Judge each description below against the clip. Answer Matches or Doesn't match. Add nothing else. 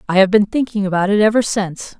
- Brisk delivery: Matches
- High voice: Matches